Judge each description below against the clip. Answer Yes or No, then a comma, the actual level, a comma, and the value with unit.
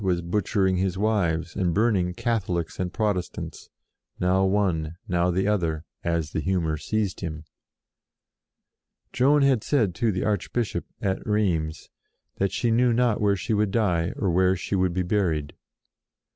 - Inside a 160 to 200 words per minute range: No, average, 150 wpm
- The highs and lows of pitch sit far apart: No, average, 3.6 semitones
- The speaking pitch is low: Yes, very low, 95 Hz